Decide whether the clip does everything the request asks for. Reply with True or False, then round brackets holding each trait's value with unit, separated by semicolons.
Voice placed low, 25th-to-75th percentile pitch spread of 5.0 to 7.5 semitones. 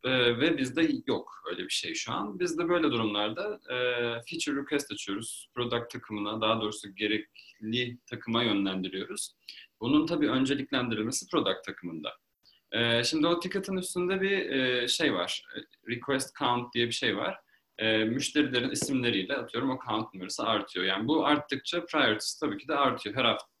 True (125 Hz; 5.5 semitones)